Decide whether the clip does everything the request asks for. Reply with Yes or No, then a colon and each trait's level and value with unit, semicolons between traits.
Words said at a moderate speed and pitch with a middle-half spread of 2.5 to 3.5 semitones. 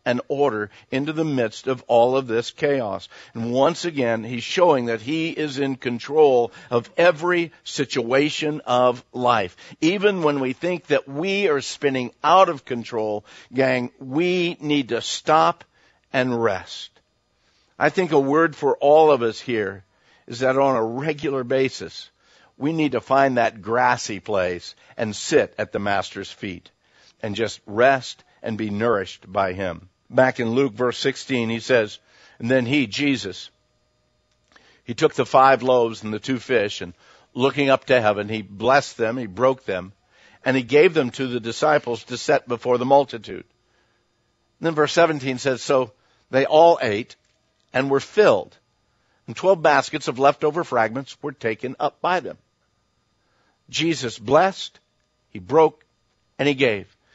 No: average, 160 wpm; average, 4.0 semitones